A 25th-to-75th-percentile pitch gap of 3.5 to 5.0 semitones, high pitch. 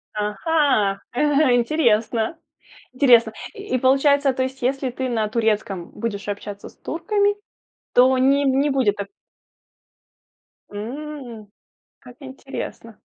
Yes: average, 4.2 semitones; very high, 250 Hz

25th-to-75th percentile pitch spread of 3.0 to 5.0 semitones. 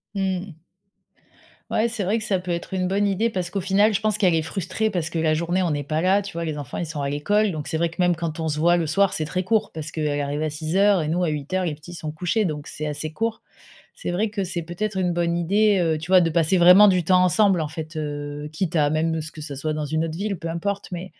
Yes: average, 3.5 semitones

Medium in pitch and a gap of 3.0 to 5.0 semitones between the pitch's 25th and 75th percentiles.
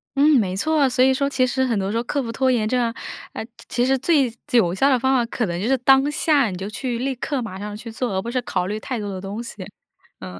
No: high, 245 Hz; average, 4.1 semitones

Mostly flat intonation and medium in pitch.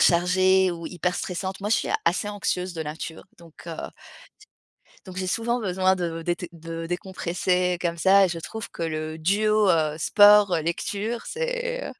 No: average, 3.2 semitones; medium, 180 Hz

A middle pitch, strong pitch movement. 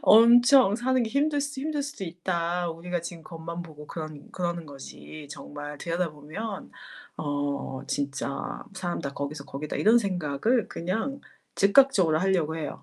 Yes: medium, 175 Hz; wide, 6.7 semitones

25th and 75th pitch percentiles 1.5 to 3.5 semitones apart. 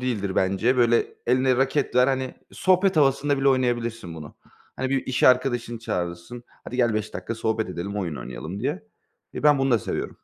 No: average, 4.3 semitones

